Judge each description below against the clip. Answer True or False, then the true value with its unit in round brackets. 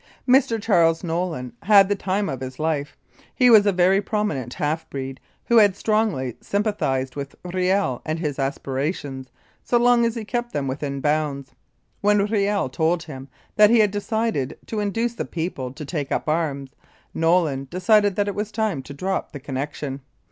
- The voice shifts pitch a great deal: True (6.9 semitones)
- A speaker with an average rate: True (175 wpm)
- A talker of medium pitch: True (175 Hz)